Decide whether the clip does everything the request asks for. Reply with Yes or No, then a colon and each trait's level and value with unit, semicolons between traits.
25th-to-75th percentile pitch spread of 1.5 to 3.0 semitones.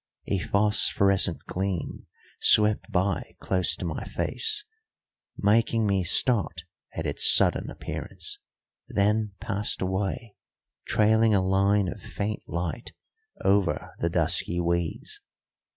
Yes: narrow, 2.6 semitones